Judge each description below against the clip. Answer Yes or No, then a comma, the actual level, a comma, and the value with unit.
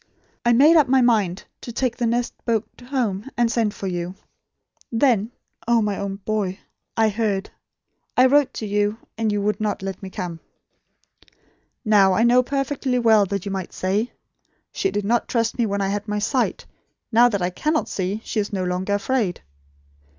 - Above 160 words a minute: Yes, average, 185 wpm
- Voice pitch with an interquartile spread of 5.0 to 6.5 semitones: No, average, 3.4 semitones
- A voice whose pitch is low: No, high, 215 Hz